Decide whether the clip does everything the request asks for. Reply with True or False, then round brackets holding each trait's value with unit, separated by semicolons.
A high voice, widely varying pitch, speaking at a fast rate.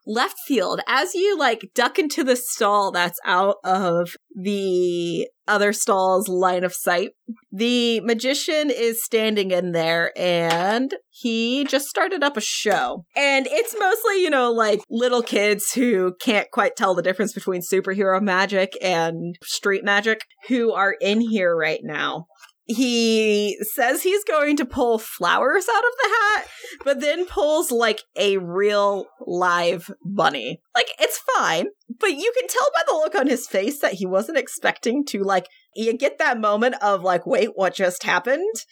False (215 Hz; 5.9 semitones; 165 wpm)